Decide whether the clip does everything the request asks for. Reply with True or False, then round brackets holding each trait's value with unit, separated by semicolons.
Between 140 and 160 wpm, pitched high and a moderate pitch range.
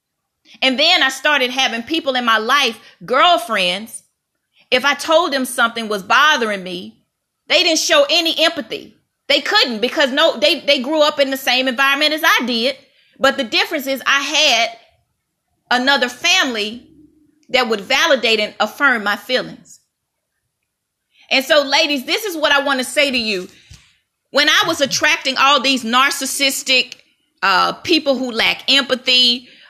True (155 wpm; 275 Hz; 3.3 semitones)